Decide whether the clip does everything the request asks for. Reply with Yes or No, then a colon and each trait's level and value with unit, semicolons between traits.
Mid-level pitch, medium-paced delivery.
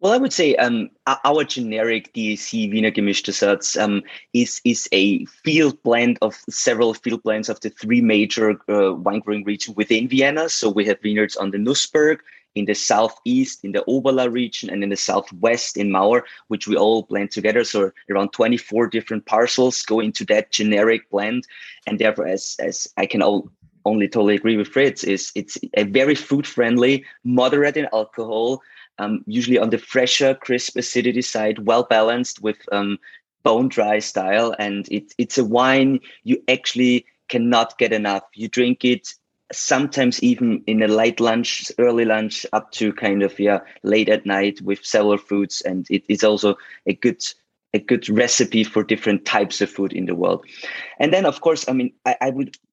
No: low, 115 Hz; average, 180 wpm